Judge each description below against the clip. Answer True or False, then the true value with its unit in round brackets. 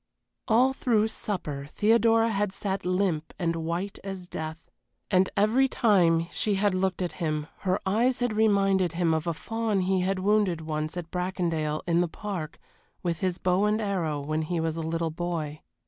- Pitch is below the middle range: False (185 Hz)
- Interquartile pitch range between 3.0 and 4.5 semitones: True (3.9 semitones)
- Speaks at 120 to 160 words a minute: False (180 wpm)